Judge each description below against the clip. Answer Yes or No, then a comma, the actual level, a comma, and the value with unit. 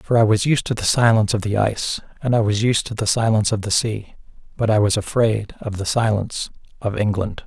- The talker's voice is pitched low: Yes, low, 110 Hz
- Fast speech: Yes, fast, 235 wpm